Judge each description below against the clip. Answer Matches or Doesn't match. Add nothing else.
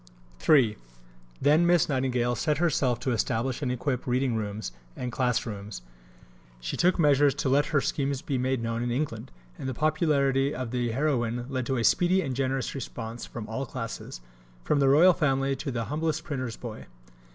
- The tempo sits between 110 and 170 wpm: Doesn't match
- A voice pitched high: Doesn't match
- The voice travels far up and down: Doesn't match